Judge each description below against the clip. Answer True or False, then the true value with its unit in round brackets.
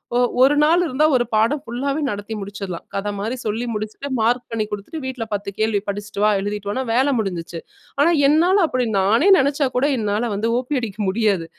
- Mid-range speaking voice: False (225 Hz)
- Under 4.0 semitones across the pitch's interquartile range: False (4.8 semitones)